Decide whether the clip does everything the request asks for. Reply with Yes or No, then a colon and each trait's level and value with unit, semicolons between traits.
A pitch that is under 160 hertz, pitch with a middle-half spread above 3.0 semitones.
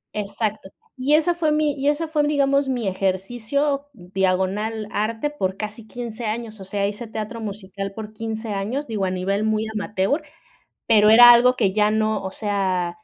No: high, 215 Hz; average, 4.0 semitones